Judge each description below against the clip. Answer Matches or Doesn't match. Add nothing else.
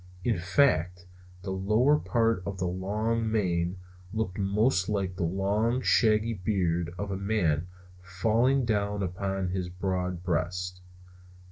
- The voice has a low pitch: Matches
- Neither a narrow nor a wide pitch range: Matches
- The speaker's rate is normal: Doesn't match